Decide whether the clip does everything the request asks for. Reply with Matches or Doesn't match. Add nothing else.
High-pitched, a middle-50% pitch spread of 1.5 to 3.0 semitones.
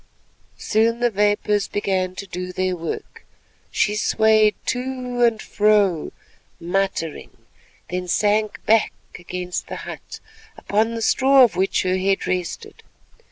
Doesn't match